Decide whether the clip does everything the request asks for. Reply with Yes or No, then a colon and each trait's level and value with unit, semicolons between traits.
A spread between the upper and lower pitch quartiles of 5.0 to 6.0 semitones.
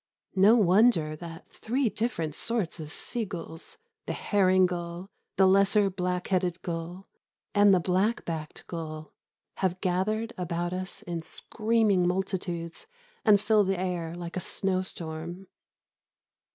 No: average, 2.8 semitones